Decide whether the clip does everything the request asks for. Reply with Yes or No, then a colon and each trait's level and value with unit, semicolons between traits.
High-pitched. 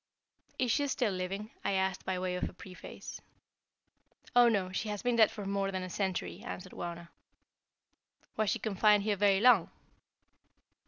Yes: high, 195 Hz